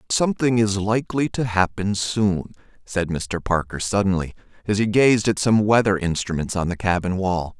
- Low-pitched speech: Yes, low, 100 Hz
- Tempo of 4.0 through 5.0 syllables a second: Yes, 4.9 syllables/s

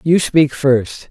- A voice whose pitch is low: No, medium, 145 Hz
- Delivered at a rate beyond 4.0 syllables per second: No, 3.0 syllables/s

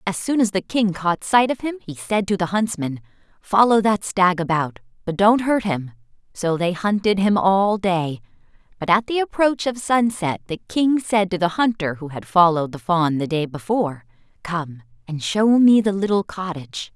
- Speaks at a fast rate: No, average, 195 wpm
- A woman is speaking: Yes, female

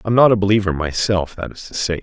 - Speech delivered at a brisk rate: Yes, fast, 265 wpm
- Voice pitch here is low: Yes, very low, 95 Hz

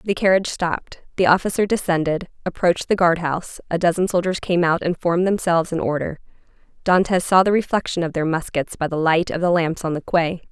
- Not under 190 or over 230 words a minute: Yes, average, 200 wpm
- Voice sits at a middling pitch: Yes, medium, 175 Hz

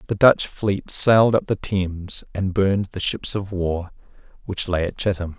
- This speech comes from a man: Yes, male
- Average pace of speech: Yes, average, 190 wpm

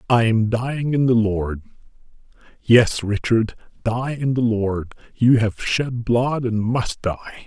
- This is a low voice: Yes, low, 115 Hz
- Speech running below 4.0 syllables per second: Yes, 3.8 syllables/s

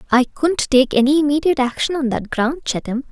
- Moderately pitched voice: No, very high, 275 Hz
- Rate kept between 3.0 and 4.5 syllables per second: No, 5.9 syllables/s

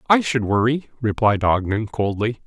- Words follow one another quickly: No, average, 145 wpm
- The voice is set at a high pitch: No, low, 115 Hz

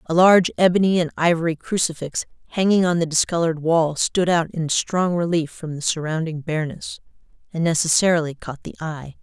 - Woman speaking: Yes, female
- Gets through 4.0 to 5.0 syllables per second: No, 5.6 syllables/s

